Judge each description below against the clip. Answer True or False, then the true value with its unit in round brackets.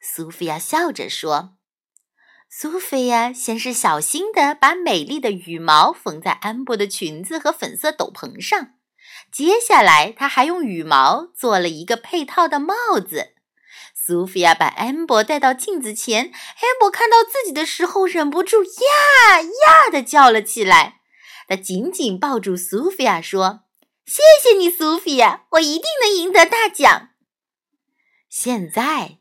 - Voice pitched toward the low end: False (290 Hz)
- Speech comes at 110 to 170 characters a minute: False (215 characters per minute)